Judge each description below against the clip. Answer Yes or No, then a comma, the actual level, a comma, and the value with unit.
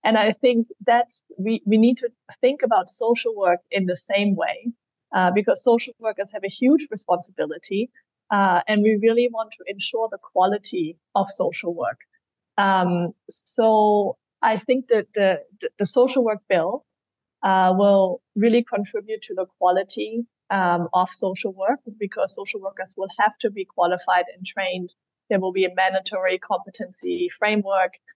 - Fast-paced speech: No, average, 160 wpm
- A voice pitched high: Yes, high, 205 Hz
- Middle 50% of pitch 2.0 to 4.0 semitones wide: Yes, average, 3.7 semitones